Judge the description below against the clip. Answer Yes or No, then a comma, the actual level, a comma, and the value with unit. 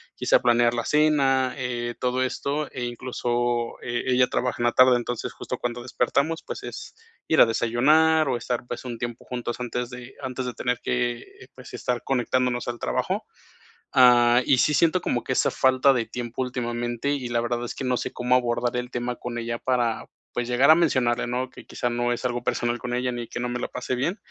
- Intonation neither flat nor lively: No, narrow, 1.2 semitones